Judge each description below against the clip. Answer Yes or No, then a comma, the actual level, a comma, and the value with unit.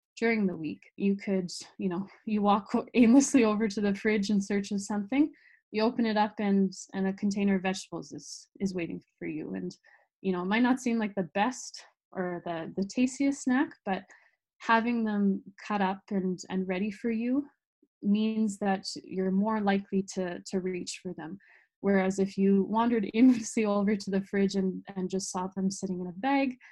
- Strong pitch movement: No, average, 2.8 semitones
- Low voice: No, high, 200 Hz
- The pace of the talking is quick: No, average, 195 wpm